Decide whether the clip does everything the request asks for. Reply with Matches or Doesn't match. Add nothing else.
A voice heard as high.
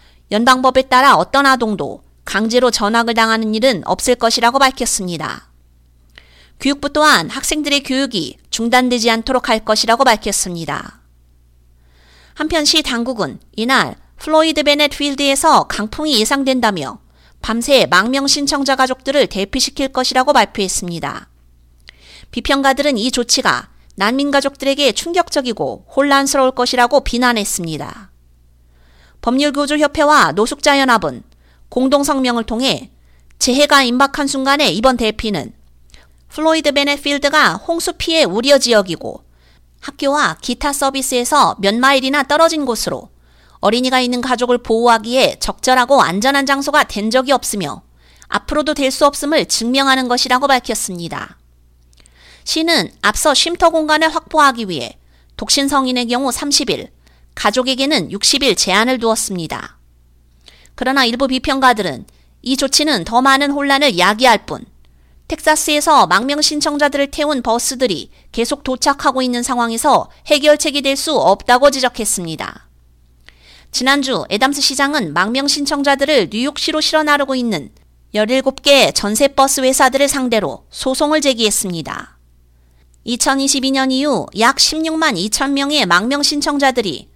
Matches